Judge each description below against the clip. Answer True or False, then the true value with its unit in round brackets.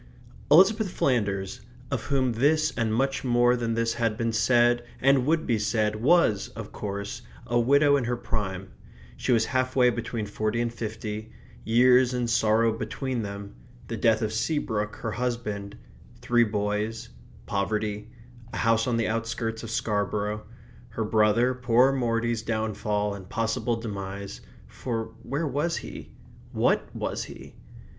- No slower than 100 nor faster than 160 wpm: True (150 wpm)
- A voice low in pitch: True (115 Hz)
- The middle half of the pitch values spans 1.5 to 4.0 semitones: True (2.6 semitones)